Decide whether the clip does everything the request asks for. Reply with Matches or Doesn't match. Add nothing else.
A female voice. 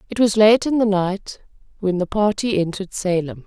Matches